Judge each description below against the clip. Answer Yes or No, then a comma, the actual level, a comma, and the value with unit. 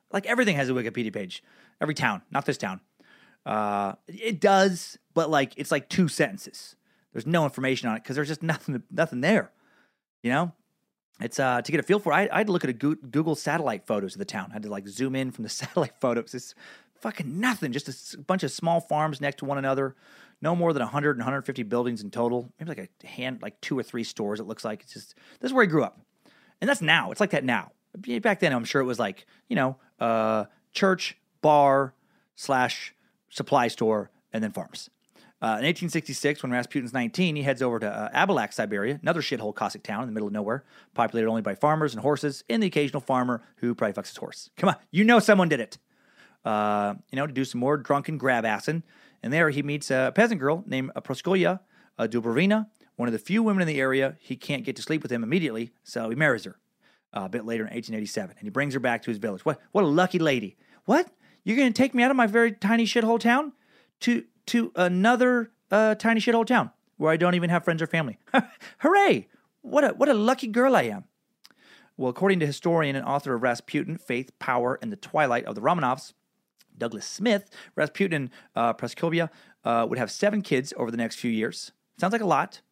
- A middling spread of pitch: No, wide, 7.7 semitones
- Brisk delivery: Yes, fast, 225 wpm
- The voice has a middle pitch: Yes, medium, 150 Hz